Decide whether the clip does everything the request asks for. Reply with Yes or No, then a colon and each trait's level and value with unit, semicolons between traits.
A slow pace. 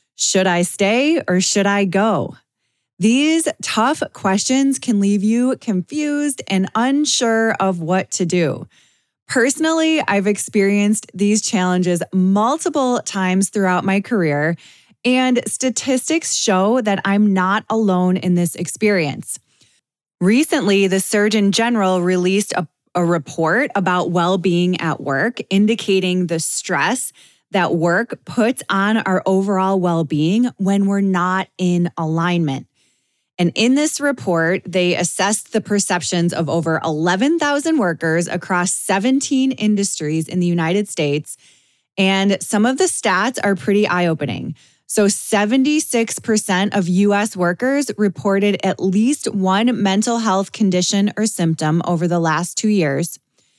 Yes: slow, 130 wpm